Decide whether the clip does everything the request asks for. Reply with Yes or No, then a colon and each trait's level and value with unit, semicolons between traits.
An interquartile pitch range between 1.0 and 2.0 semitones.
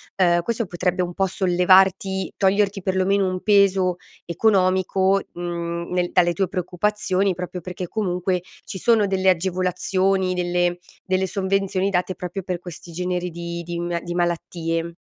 Yes: narrow, 1.7 semitones